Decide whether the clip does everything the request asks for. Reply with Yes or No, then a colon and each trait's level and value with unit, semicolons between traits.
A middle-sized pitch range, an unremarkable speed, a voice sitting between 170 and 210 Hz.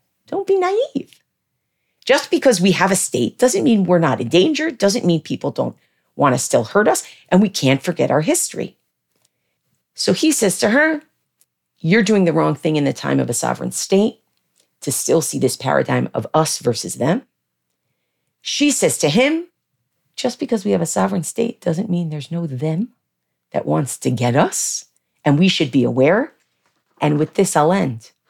No: wide, 8.0 semitones; average, 185 wpm; high, 190 Hz